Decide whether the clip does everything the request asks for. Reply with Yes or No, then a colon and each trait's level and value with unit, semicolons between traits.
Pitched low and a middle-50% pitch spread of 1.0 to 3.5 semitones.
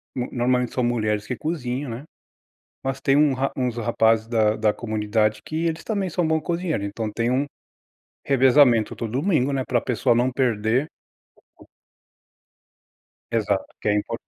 No: low, 125 Hz; average, 3.9 semitones